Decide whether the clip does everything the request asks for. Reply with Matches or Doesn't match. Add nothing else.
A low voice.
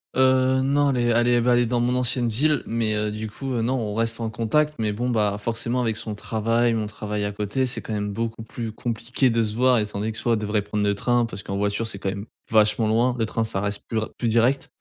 Matches